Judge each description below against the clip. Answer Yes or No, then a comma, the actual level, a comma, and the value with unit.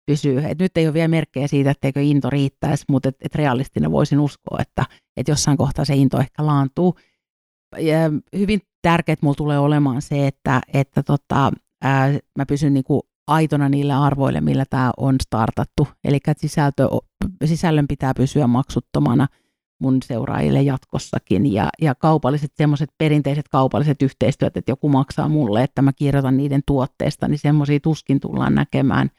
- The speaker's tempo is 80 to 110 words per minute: No, average, 150 wpm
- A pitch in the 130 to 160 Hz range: Yes, medium, 140 Hz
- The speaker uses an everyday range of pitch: No, narrow, 2.0 semitones